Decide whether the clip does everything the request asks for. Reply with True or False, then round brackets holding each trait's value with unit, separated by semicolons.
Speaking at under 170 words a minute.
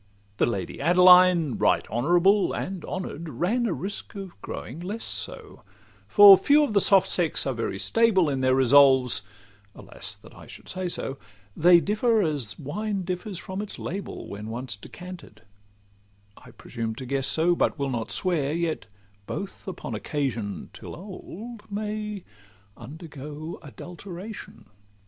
True (140 wpm)